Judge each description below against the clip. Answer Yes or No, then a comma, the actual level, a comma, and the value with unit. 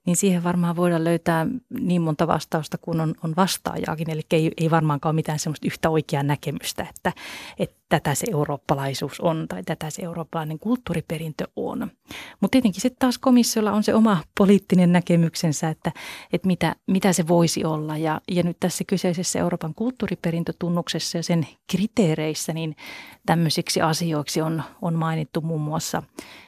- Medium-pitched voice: Yes, medium, 170 Hz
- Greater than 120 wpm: Yes, fast, 155 wpm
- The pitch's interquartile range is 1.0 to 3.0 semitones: Yes, average, 2.7 semitones